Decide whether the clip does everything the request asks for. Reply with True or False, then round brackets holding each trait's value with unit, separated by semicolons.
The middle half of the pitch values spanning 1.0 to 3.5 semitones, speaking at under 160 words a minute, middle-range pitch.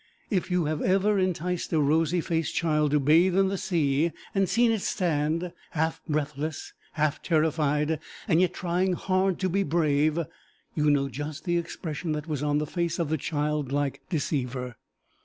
False (3.1 semitones; 170 wpm; 160 Hz)